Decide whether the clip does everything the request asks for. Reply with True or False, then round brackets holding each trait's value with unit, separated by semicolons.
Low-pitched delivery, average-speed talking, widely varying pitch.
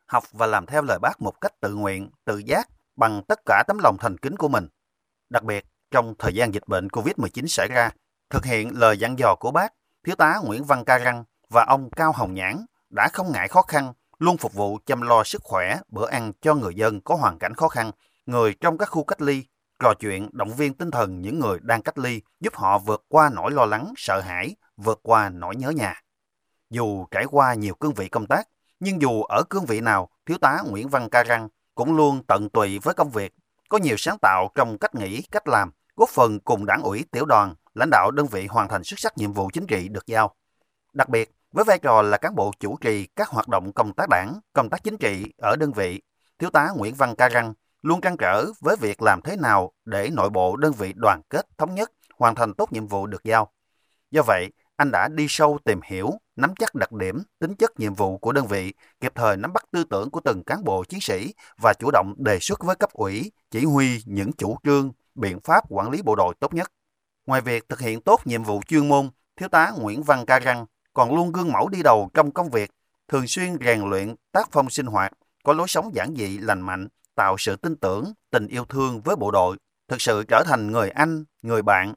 True (120 Hz; 235 wpm; 6.3 semitones)